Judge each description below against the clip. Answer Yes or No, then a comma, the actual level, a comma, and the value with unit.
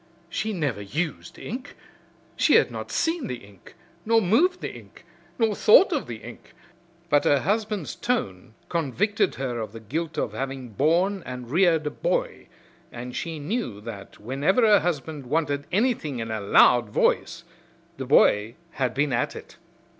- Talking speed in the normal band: Yes, average, 160 wpm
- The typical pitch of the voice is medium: Yes, medium, 150 Hz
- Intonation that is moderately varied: No, wide, 8.5 semitones